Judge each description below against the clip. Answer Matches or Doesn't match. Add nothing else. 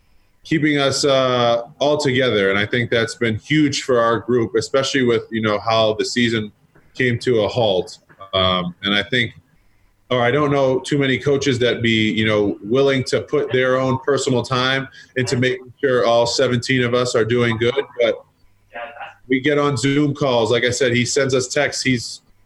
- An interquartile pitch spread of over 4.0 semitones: Doesn't match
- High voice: Doesn't match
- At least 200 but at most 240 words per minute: Doesn't match